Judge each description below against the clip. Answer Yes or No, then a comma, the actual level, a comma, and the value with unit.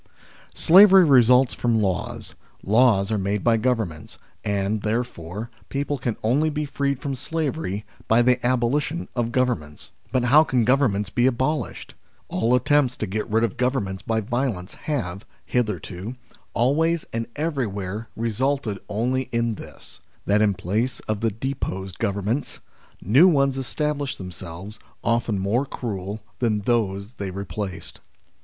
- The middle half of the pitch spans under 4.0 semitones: No, average, 4.5 semitones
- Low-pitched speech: Yes, low, 115 Hz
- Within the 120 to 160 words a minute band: Yes, average, 140 wpm